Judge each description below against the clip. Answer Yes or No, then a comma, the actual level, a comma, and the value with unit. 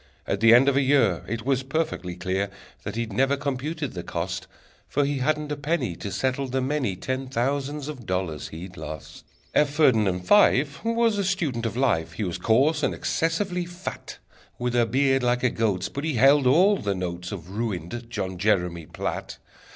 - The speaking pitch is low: Yes, low, 125 Hz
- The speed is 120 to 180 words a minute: No, average, 190 wpm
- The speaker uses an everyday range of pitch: No, wide, 6.9 semitones